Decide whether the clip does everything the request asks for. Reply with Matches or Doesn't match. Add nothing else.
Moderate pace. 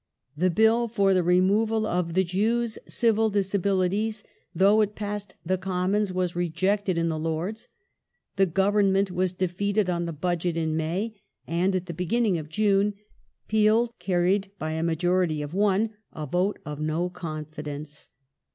Matches